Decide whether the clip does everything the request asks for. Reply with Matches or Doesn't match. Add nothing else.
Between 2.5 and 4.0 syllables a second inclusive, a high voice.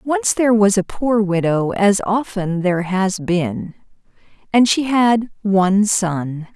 Matches